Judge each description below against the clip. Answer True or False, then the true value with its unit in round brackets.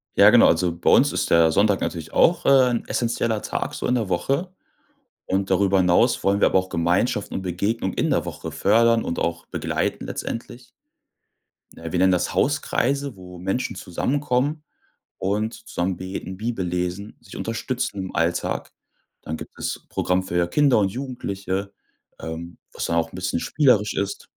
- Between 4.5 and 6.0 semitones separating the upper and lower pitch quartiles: True (4.8 semitones)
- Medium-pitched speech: False (100 Hz)